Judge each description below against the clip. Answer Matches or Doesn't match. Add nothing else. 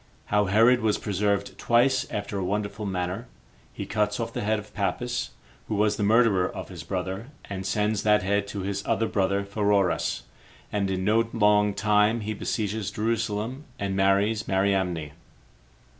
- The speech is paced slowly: Doesn't match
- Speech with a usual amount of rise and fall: Doesn't match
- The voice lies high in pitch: Doesn't match